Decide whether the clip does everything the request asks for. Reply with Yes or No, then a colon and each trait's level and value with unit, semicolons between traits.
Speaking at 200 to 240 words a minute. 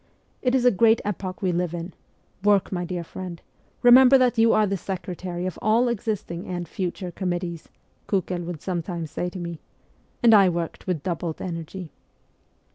No: average, 170 wpm